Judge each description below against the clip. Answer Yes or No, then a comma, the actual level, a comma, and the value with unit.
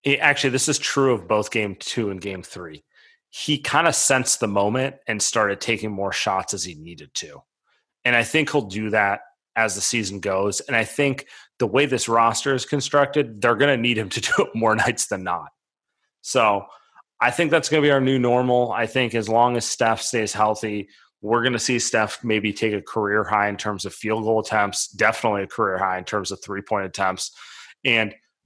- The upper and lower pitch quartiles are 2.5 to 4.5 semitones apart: Yes, average, 3.9 semitones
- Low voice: Yes, low, 115 Hz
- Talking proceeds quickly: Yes, fast, 215 wpm